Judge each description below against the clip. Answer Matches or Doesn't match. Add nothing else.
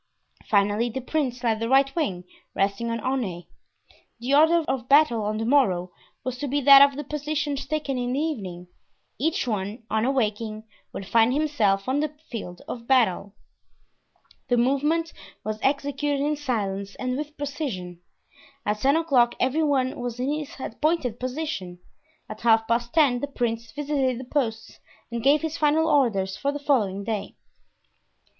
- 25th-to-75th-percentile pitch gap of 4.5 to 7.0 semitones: Matches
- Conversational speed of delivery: Matches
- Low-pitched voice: Doesn't match